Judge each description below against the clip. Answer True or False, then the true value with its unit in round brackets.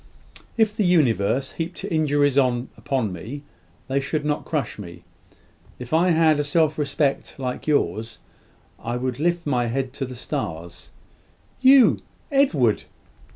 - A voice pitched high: False (140 Hz)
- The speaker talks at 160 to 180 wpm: False (135 wpm)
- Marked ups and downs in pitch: False (4.5 semitones)